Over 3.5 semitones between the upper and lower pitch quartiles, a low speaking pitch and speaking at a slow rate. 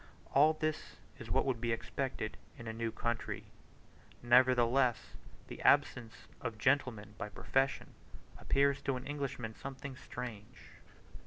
No: average, 3.0 semitones; low, 125 Hz; slow, 130 wpm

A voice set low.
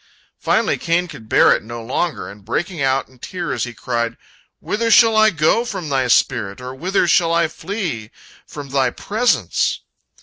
No: medium, 150 Hz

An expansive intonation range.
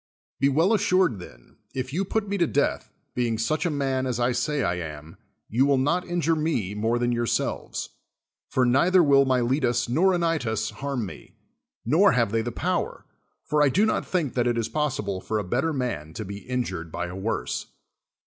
Yes: wide, 5.7 semitones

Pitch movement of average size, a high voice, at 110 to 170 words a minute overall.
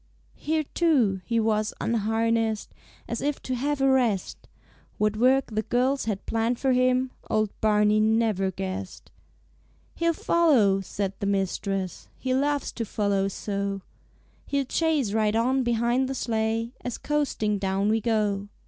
Yes: average, 4.1 semitones; high, 225 Hz; average, 145 wpm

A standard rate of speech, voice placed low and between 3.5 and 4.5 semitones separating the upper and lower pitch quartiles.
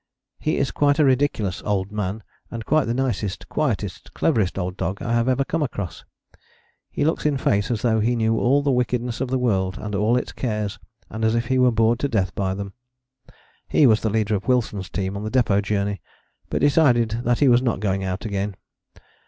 No: fast, 215 wpm; low, 110 Hz; average, 4.0 semitones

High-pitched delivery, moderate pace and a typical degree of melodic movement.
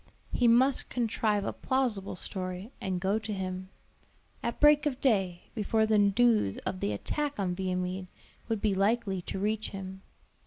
Yes: high, 205 Hz; average, 160 wpm; average, 3.7 semitones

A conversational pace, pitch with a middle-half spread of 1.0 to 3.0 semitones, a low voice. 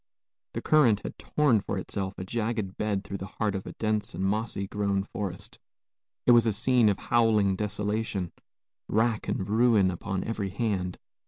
Yes: average, 170 wpm; narrow, 2.6 semitones; low, 105 Hz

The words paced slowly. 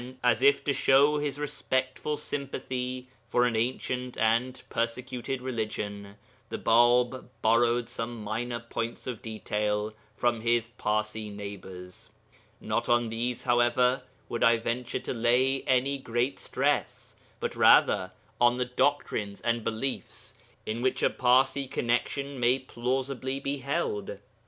Yes: slow, 130 wpm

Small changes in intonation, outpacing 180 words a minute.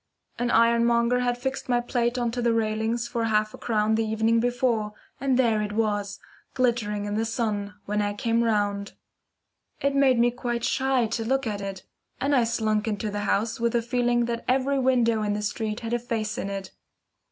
Yes: narrow, 2.3 semitones; average, 200 wpm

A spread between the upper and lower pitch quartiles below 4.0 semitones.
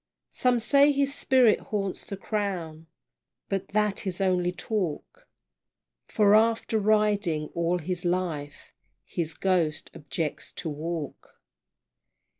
No: average, 4.4 semitones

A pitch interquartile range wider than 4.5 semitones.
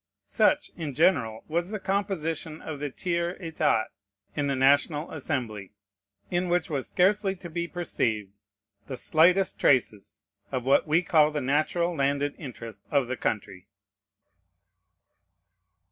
Yes: average, 4.9 semitones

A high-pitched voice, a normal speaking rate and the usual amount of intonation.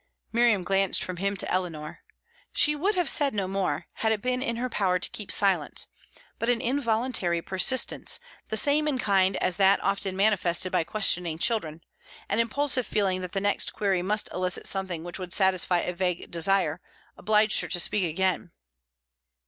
Yes: high, 195 Hz; average, 175 wpm; average, 3.6 semitones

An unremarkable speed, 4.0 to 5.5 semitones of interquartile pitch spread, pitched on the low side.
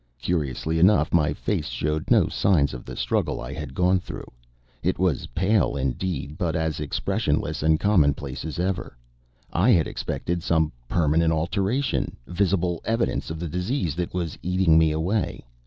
No: average, 160 wpm; average, 3.2 semitones; very low, 85 Hz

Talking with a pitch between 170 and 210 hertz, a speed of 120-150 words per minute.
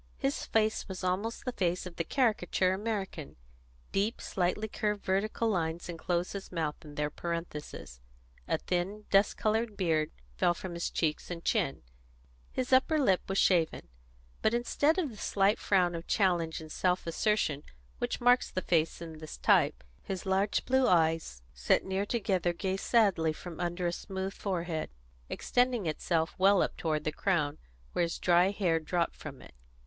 No: medium, 185 Hz; average, 165 wpm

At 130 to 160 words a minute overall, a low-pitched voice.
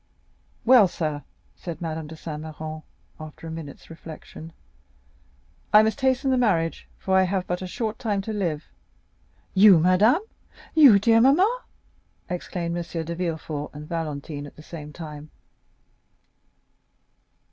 No: average, 140 wpm; medium, 170 Hz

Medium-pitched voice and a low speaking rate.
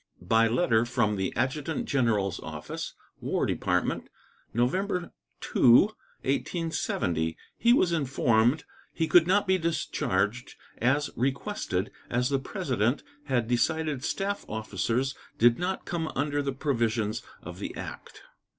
No: low, 130 Hz; slow, 125 wpm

